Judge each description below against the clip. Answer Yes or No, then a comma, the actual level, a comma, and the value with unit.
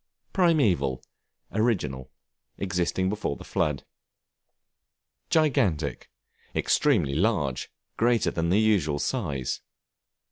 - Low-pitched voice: Yes, very low, 90 Hz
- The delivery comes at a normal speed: No, slow, 80 wpm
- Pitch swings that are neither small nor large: No, wide, 7.6 semitones